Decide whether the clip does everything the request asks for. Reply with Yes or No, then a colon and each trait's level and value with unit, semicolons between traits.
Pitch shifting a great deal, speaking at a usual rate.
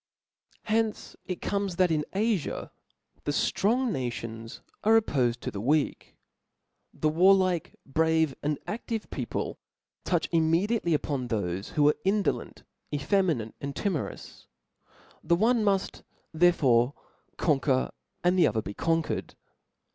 No: wide, 6.2 semitones; slow, 125 wpm